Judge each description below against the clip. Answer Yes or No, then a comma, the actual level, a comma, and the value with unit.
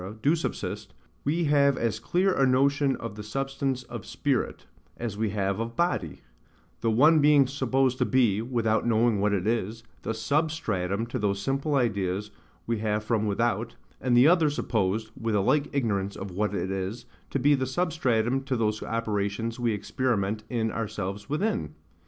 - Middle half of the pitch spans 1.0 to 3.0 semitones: No, average, 4.4 semitones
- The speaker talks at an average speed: Yes, average, 170 wpm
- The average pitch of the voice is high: No, low, 115 Hz